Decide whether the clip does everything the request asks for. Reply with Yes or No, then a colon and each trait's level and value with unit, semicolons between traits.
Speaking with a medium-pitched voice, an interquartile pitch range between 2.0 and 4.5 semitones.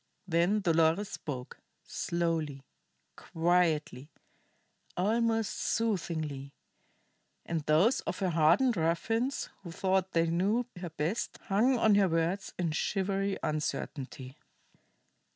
Yes: medium, 175 Hz; average, 4.0 semitones